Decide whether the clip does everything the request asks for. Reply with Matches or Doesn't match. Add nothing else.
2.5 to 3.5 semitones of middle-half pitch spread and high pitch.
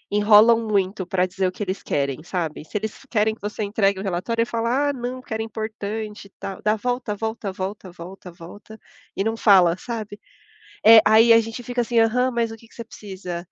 Matches